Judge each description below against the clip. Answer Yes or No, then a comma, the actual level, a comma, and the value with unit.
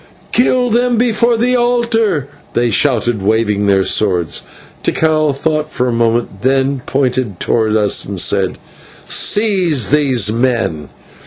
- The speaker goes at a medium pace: No, slow, 130 wpm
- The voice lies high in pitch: No, low, 130 Hz